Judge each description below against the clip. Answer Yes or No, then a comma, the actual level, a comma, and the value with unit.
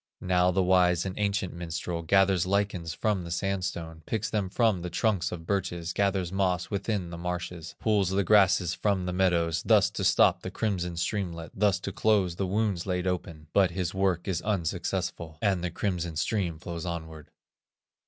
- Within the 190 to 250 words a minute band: No, average, 175 wpm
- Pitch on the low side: Yes, very low, 90 Hz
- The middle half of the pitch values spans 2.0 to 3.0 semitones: Yes, narrow, 2.5 semitones